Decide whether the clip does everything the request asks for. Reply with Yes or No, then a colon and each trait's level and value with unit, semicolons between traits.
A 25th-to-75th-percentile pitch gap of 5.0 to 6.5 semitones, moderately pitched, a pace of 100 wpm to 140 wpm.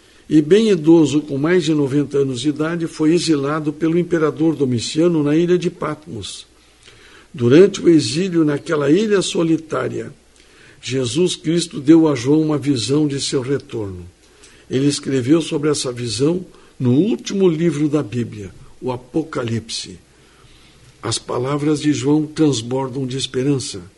No: average, 3.5 semitones; medium, 150 Hz; average, 135 wpm